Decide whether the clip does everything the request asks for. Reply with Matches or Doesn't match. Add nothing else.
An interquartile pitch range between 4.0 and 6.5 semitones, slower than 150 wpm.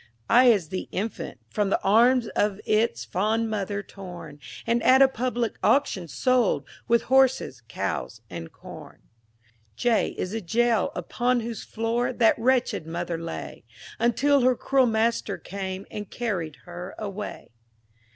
Matches